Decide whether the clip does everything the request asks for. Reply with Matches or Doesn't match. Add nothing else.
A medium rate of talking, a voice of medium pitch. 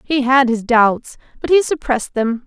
Doesn't match